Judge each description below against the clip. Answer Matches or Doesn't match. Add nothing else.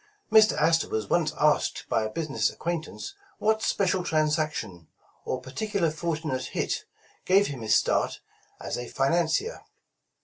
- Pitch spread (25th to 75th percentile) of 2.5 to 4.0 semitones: Doesn't match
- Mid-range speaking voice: Matches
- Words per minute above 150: Doesn't match